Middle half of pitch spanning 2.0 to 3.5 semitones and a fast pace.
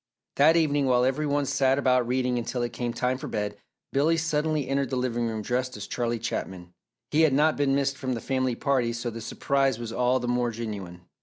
Yes: average, 2.8 semitones; fast, 220 wpm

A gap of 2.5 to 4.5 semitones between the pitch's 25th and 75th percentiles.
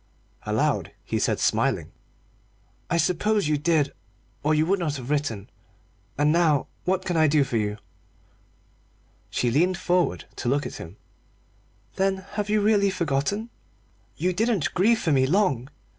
No: average, 5.0 semitones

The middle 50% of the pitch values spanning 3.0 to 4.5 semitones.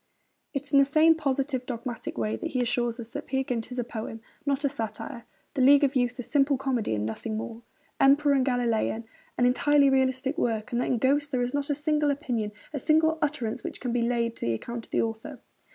Yes: average, 3.3 semitones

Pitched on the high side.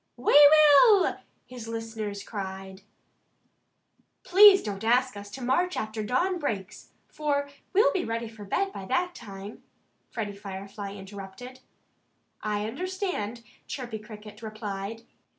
Yes: high, 225 Hz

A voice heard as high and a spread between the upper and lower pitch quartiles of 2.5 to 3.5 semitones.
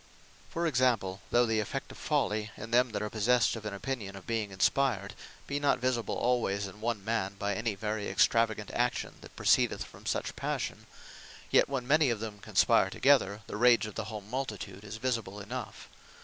No: low, 110 Hz; average, 3.2 semitones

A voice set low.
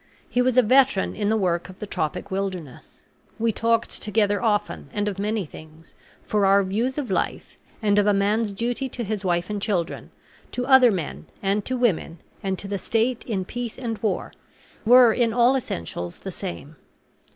No: high, 210 Hz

